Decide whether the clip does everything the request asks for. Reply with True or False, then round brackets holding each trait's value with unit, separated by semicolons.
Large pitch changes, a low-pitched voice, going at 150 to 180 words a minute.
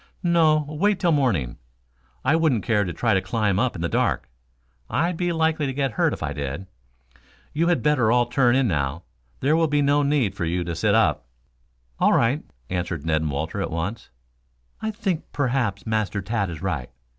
False (8.9 semitones; 115 Hz; 195 wpm)